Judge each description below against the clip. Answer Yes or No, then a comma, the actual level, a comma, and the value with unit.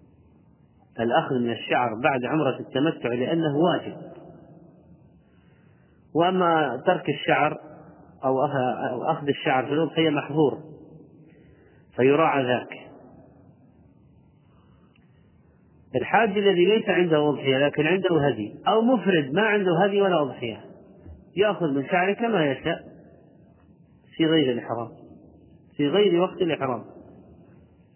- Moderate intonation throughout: Yes, average, 4.0 semitones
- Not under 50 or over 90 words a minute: No, average, 100 wpm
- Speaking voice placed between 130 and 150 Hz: No, medium, 160 Hz